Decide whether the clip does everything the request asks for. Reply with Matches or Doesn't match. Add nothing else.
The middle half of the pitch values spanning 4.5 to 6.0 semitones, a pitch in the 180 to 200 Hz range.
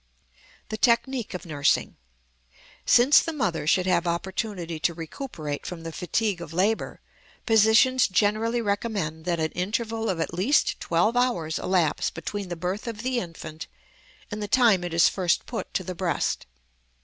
Matches